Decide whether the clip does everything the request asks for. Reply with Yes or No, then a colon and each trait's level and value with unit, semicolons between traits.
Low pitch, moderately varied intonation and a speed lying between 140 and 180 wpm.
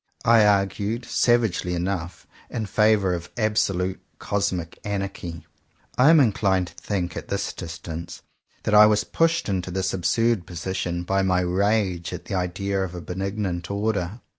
Yes: very low, 95 Hz; average, 3.0 semitones; average, 150 wpm